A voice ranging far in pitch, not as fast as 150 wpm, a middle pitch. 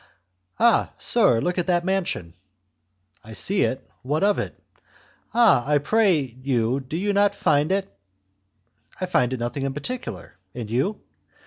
Yes: wide, 7.8 semitones; average, 140 wpm; medium, 150 Hz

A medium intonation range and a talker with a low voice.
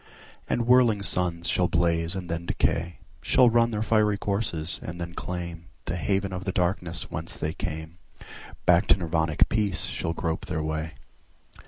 Yes: average, 3.1 semitones; very low, 85 Hz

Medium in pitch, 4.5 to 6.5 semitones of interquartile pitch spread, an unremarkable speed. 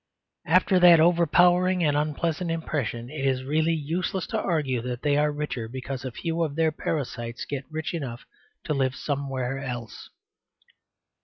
No: medium, 150 Hz; average, 4.0 semitones; average, 155 wpm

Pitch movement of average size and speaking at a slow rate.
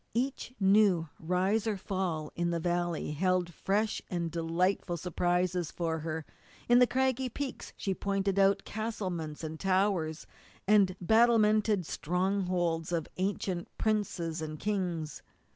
Yes: average, 3.5 semitones; slow, 125 wpm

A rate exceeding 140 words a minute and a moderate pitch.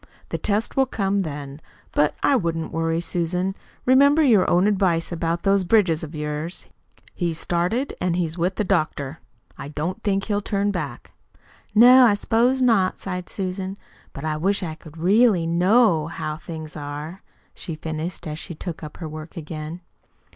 Yes: average, 170 wpm; medium, 175 Hz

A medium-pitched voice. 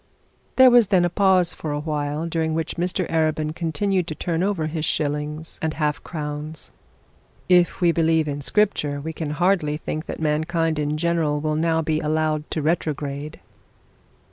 Yes: medium, 160 Hz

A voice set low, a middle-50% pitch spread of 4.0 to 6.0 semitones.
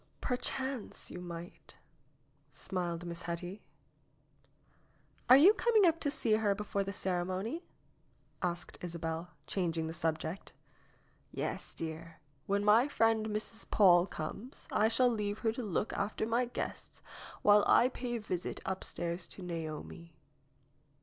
No: high, 200 Hz; average, 4.8 semitones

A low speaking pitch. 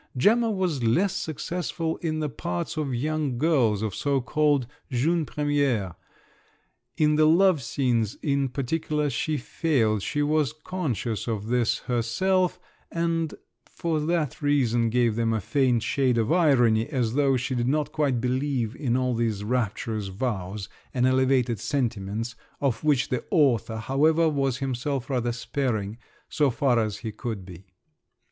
Yes: low, 130 Hz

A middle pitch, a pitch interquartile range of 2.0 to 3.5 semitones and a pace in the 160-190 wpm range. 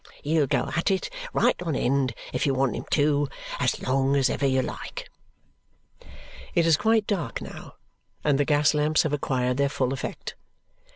Yes: medium, 145 Hz; narrow, 2.6 semitones; average, 175 wpm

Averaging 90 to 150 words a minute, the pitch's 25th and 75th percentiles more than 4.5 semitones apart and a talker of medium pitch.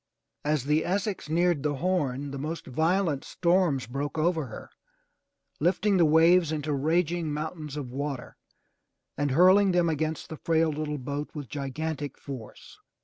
No: average, 145 wpm; average, 3.0 semitones; medium, 155 Hz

